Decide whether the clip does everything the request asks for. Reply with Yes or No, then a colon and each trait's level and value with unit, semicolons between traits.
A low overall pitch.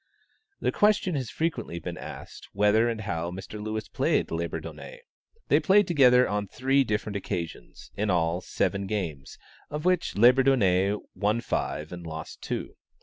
Yes: low, 105 Hz